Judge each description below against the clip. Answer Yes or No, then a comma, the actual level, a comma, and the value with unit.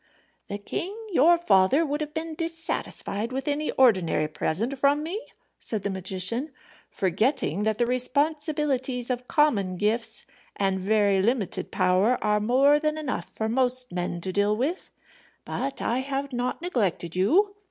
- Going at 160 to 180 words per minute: No, average, 150 wpm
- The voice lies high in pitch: Yes, very high, 250 Hz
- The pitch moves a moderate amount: No, wide, 6.5 semitones